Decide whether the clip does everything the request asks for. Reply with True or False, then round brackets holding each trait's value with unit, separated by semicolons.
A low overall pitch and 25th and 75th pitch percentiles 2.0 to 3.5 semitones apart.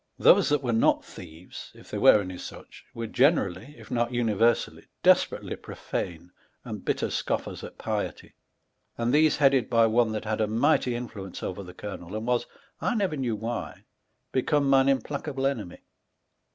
False (115 Hz; 4.5 semitones)